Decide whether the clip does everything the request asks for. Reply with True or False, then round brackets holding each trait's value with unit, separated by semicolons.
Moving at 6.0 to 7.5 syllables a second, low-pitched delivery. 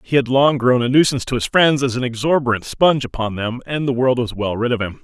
True (6.1 syllables/s; 125 Hz)